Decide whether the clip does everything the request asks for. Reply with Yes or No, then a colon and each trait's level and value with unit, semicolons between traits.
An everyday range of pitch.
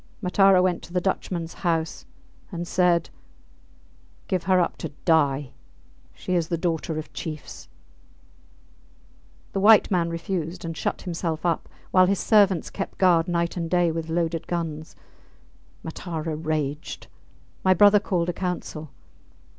No: narrow, 2.1 semitones